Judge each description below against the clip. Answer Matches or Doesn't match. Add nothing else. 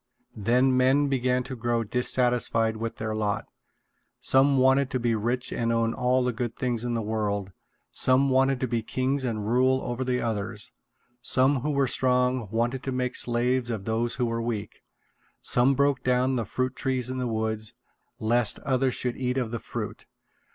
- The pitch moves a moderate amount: Doesn't match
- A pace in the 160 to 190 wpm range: Matches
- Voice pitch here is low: Matches